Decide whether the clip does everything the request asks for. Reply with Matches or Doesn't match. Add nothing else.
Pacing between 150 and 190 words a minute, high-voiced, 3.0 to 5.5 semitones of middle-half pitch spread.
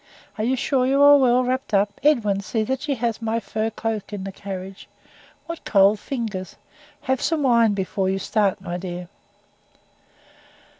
Matches